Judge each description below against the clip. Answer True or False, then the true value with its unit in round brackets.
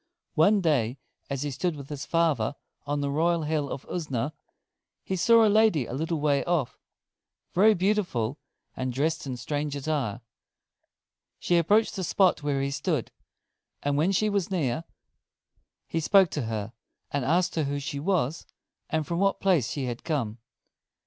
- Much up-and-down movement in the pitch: False (4.2 semitones)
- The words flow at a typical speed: True (160 wpm)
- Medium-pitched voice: True (150 Hz)